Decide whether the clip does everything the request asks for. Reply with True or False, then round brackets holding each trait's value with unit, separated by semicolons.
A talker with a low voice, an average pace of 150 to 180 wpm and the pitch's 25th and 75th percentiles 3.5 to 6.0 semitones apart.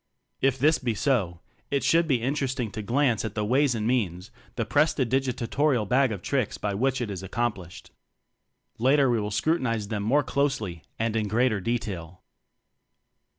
True (120 Hz; 165 wpm; 4.3 semitones)